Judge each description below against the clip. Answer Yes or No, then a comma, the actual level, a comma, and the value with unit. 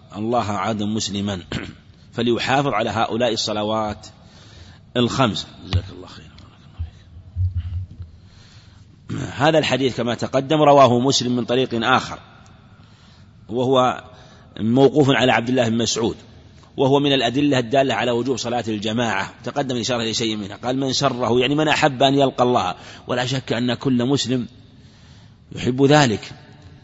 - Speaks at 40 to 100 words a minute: No, average, 125 wpm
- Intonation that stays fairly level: No, average, 3.8 semitones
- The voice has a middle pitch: No, low, 120 Hz